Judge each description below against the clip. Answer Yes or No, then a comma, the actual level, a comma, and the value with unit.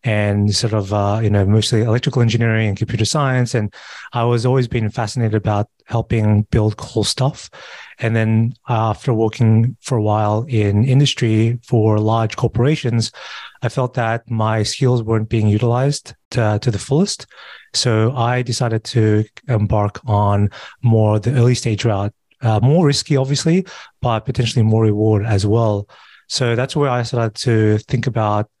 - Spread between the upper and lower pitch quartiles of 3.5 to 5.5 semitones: No, narrow, 2.4 semitones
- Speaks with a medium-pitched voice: No, low, 115 Hz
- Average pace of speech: Yes, average, 165 wpm